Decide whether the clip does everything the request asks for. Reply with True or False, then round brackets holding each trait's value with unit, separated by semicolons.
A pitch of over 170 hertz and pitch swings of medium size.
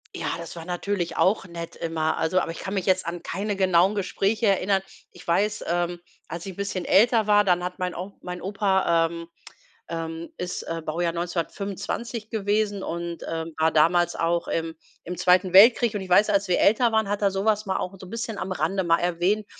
True (185 Hz; 3.0 semitones)